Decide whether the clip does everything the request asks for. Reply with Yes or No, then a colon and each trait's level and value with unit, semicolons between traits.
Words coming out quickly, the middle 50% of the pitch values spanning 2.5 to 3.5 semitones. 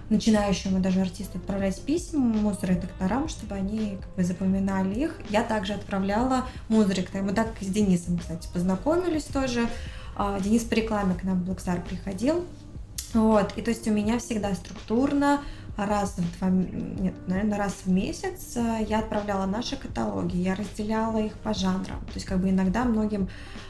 Yes: fast, 165 wpm; average, 2.9 semitones